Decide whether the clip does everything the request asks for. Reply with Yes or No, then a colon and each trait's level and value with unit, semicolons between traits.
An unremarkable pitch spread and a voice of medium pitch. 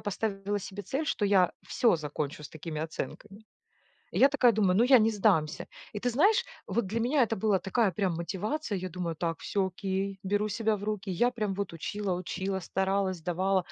No: average, 3.1 semitones; high, 195 Hz